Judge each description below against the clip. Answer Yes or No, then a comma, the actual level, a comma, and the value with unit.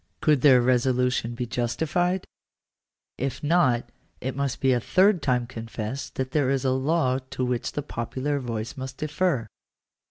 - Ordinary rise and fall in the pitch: Yes, average, 3.1 semitones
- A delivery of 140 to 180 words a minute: Yes, average, 155 wpm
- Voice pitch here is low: Yes, low, 130 Hz